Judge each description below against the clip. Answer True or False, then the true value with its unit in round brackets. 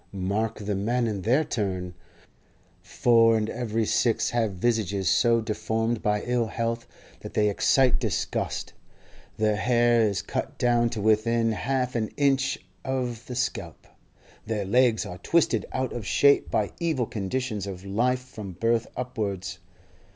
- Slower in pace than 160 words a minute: True (145 wpm)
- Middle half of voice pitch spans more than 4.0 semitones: False (2.8 semitones)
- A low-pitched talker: True (115 Hz)